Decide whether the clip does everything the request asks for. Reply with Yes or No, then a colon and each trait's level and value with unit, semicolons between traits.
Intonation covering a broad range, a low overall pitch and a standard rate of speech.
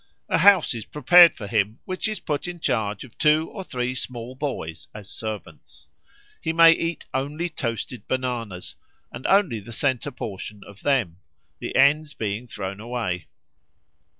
Yes: wide, 6.1 semitones; low, 125 Hz; average, 155 wpm